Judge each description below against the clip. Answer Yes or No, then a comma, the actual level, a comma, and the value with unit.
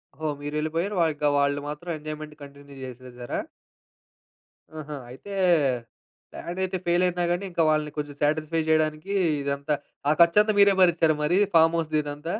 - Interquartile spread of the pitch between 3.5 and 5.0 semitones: No, narrow, 2.6 semitones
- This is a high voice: No, medium, 155 Hz